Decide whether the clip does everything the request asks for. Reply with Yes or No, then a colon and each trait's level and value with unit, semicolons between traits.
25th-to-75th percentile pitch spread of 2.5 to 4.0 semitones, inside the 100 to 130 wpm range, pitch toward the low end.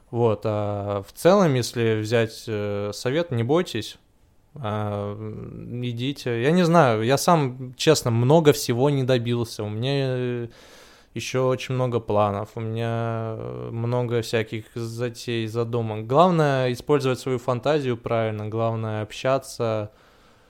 Yes: average, 3.0 semitones; average, 115 wpm; low, 120 Hz